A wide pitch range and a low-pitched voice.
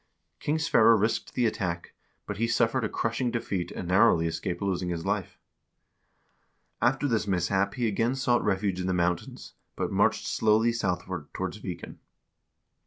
No: average, 4.3 semitones; low, 100 Hz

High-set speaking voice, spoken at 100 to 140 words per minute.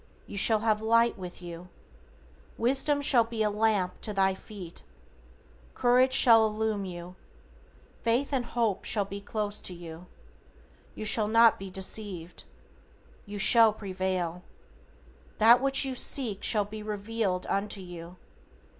Yes: high, 210 Hz; slow, 135 wpm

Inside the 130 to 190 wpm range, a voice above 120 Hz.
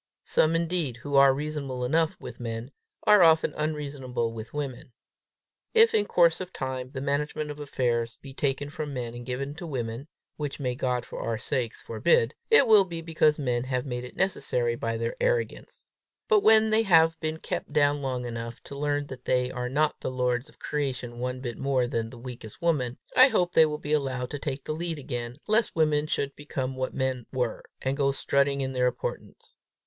No: average, 200 wpm; medium, 140 Hz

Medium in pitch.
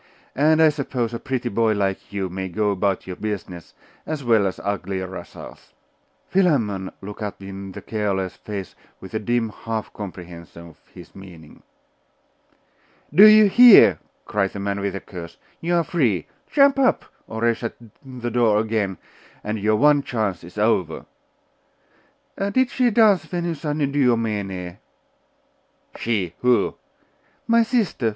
No: low, 110 Hz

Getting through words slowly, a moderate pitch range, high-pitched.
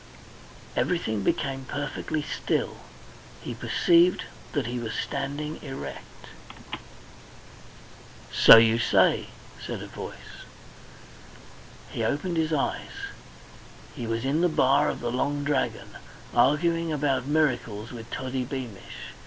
No: slow, 110 wpm; average, 3.9 semitones; low, 135 Hz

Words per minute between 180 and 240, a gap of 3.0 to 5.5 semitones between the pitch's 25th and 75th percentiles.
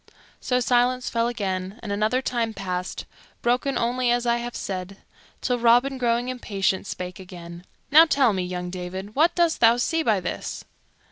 No: average, 165 wpm; average, 4.8 semitones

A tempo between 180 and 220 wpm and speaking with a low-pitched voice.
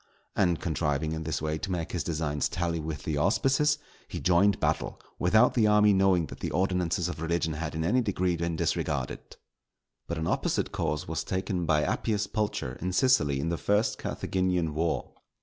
Yes: average, 185 wpm; very low, 85 Hz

